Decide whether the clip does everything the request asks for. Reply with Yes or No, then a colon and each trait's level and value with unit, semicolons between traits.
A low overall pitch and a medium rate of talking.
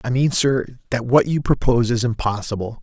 Yes: low, 120 Hz; average, 190 wpm